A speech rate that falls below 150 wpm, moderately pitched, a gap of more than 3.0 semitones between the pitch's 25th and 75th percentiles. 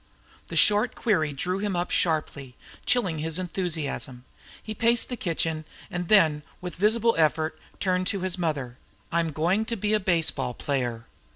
No: average, 170 wpm; medium, 175 Hz; average, 4.7 semitones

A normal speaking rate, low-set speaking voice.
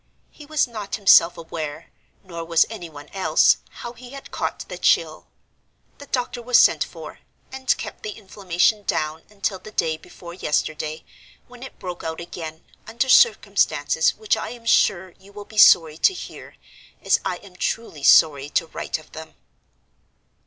No: average, 165 wpm; high, 190 Hz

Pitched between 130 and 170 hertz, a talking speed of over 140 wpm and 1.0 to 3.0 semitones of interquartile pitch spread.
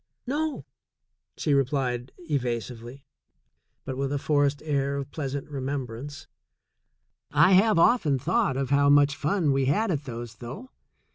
No: medium, 140 Hz; slow, 135 wpm; narrow, 2.4 semitones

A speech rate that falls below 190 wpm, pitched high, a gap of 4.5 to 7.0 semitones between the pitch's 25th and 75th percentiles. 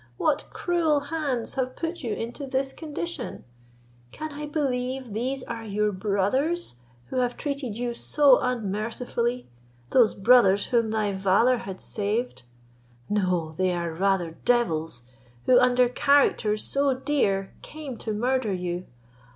Yes: slow, 135 wpm; high, 240 Hz; average, 5.1 semitones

